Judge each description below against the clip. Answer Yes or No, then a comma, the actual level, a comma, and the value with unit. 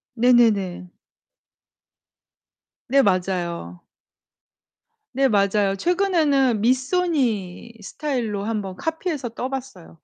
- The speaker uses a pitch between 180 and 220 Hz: No, high, 230 Hz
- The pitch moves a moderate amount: No, wide, 5.8 semitones